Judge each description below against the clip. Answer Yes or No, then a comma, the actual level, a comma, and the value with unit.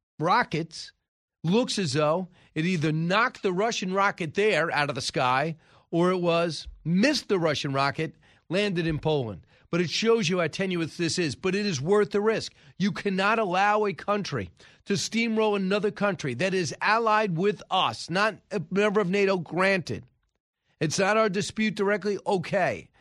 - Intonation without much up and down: No, average, 4.4 semitones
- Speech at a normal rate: Yes, average, 170 wpm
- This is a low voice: No, high, 190 Hz